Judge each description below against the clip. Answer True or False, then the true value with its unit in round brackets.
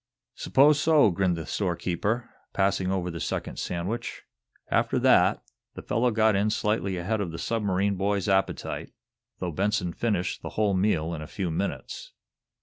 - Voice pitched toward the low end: True (100 Hz)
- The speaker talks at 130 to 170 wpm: True (155 wpm)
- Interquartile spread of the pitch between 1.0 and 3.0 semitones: False (3.4 semitones)